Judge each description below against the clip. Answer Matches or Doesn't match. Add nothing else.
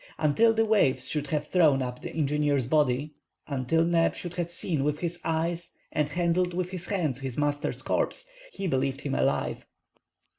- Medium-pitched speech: Matches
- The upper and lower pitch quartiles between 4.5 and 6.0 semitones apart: Doesn't match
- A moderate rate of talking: Matches